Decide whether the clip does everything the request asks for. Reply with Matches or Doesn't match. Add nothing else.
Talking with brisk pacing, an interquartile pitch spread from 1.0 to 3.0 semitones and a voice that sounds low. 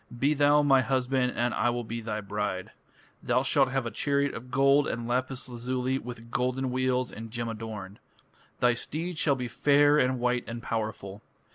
Doesn't match